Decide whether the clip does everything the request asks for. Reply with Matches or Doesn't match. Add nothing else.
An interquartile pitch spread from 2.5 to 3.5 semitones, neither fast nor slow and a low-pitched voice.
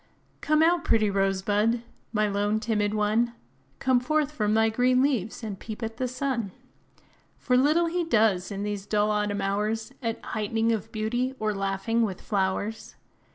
Doesn't match